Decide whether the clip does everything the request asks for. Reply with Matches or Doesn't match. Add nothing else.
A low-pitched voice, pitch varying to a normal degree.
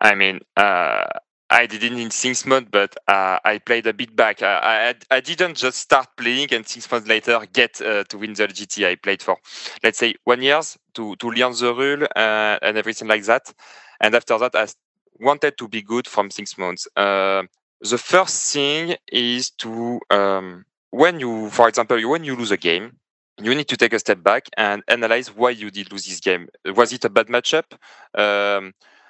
Matches